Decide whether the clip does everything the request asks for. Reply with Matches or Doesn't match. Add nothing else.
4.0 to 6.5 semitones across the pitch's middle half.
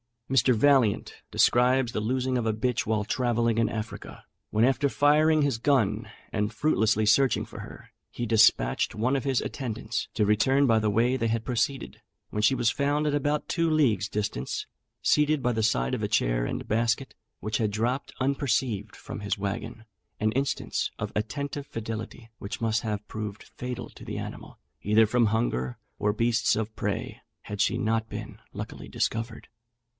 Doesn't match